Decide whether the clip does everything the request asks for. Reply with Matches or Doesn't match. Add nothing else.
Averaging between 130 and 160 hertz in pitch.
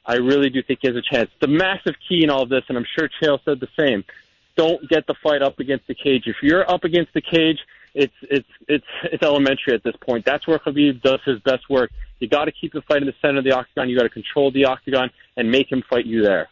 Matches